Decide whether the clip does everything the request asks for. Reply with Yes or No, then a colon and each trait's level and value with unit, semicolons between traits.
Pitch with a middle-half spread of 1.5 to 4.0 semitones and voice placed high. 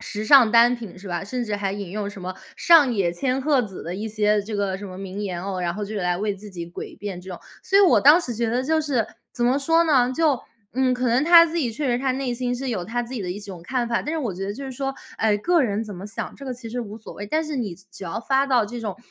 No: average, 4.8 semitones; high, 230 Hz